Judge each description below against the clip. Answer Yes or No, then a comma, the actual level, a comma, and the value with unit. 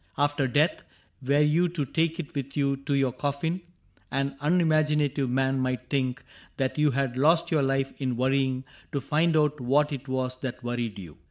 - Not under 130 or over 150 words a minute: No, average, 180 wpm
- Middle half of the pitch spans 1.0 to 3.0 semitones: Yes, narrow, 2.5 semitones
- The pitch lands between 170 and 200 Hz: No, medium, 140 Hz